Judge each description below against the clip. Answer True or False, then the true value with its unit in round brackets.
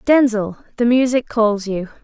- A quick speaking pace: False (145 wpm)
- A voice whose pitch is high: True (230 Hz)